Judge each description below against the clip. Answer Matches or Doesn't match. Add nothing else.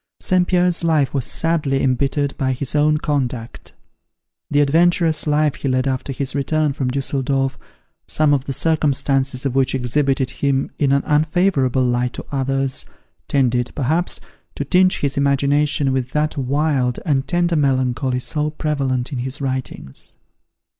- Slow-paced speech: Doesn't match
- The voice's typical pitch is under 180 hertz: Matches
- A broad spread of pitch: Doesn't match